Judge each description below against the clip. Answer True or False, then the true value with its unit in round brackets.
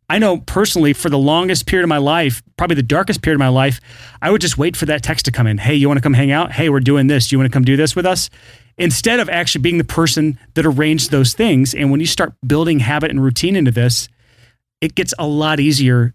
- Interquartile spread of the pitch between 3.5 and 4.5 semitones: True (3.9 semitones)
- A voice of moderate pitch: True (150 Hz)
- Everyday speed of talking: False (255 wpm)